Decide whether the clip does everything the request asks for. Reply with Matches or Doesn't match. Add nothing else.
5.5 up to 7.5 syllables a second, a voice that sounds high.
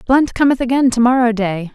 Matches